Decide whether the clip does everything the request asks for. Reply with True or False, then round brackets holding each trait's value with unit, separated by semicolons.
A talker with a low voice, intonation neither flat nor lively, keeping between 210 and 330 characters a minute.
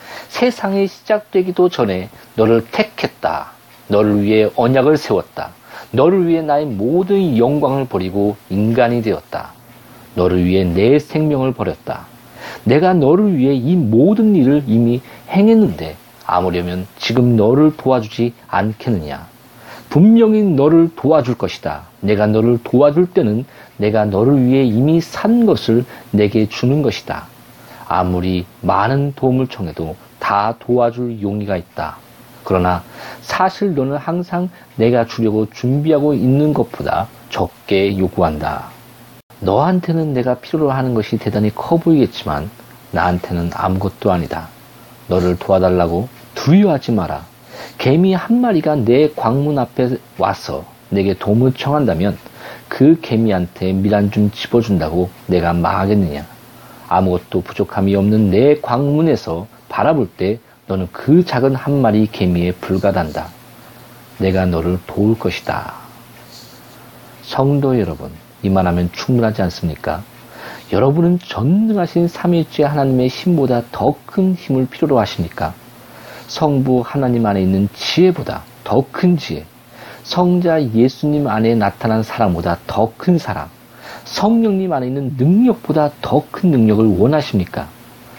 False (120 Hz; 6.4 semitones; 280 characters per minute)